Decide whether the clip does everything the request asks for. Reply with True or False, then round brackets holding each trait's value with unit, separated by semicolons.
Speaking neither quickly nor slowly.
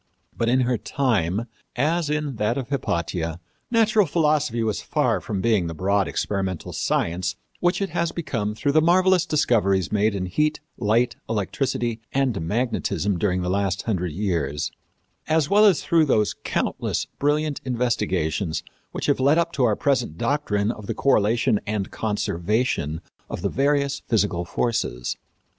True (150 wpm)